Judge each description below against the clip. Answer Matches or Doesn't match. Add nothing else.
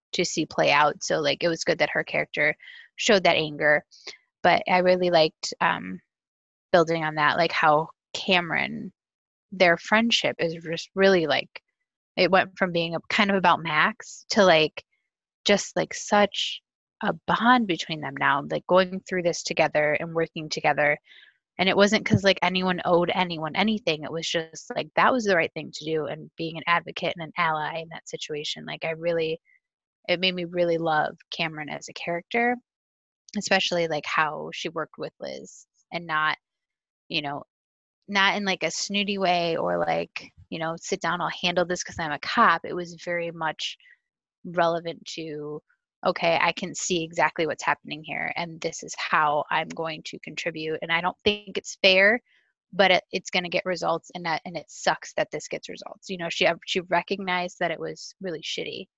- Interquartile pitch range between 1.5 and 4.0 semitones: Matches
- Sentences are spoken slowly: Doesn't match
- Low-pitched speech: Doesn't match